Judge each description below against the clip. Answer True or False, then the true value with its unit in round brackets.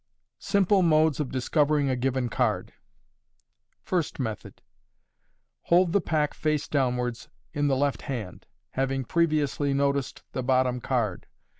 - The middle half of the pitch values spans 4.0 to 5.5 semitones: False (3.2 semitones)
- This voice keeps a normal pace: False (130 wpm)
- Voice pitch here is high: False (140 Hz)